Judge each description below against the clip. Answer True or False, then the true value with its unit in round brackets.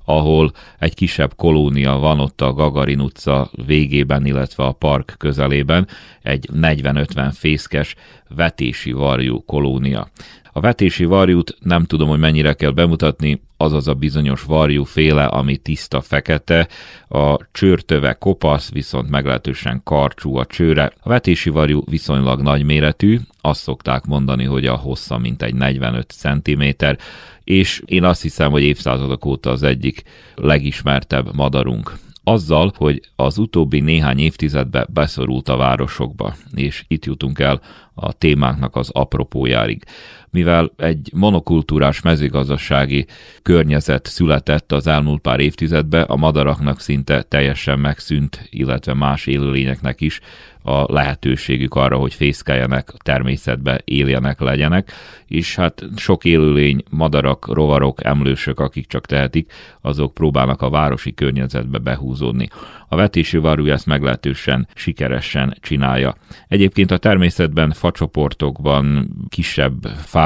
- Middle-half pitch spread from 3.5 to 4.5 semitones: False (2.8 semitones)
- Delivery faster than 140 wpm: False (125 wpm)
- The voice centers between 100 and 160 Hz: False (70 Hz)